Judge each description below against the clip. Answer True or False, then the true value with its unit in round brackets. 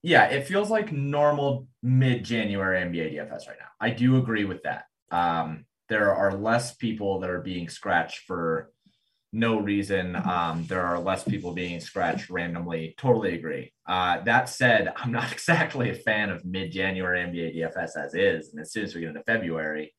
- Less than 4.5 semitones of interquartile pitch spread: False (5.2 semitones)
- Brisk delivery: False (185 wpm)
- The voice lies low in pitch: True (95 Hz)